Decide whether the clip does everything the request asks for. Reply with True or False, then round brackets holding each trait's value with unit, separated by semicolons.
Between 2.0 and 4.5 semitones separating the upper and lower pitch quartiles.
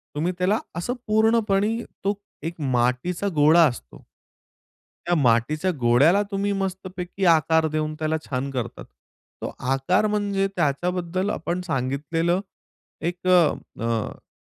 False (4.9 semitones)